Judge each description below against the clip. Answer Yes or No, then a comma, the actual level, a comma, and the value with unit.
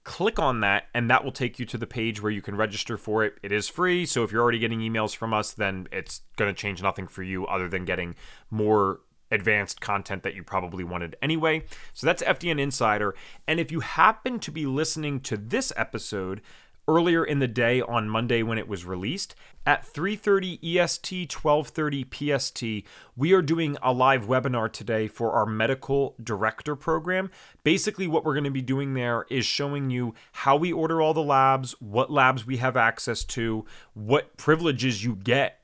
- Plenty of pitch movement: Yes, wide, 5.7 semitones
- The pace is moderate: Yes, average, 195 wpm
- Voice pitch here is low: Yes, low, 125 Hz